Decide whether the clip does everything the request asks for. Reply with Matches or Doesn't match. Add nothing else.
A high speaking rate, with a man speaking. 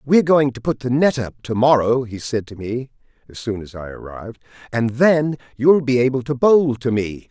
Matches